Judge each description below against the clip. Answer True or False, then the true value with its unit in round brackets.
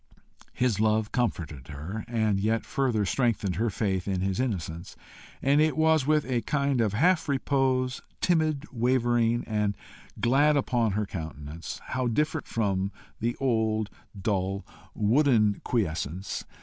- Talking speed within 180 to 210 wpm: False (135 wpm)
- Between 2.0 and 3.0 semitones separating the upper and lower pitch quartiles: False (4.9 semitones)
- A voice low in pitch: True (115 Hz)